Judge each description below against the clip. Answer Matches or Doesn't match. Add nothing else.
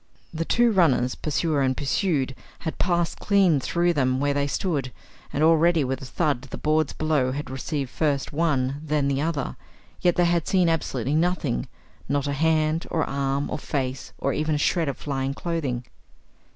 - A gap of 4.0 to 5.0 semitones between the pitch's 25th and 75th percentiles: Doesn't match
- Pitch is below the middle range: Doesn't match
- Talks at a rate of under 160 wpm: Doesn't match